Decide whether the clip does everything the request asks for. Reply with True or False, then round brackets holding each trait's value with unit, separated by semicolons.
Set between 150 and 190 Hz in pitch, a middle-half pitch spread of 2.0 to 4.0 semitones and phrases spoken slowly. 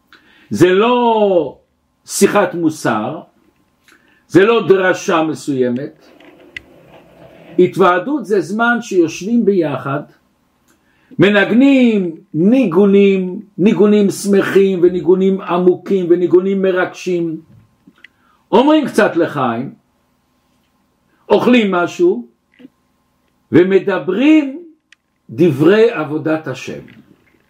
True (185 Hz; 3.5 semitones; 65 wpm)